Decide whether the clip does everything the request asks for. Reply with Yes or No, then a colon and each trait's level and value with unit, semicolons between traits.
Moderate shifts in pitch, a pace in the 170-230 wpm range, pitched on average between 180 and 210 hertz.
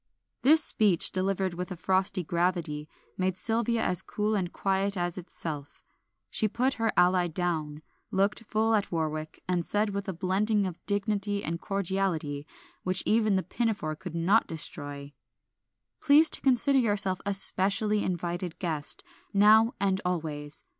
No: average, 3.5 semitones; average, 145 wpm; high, 190 Hz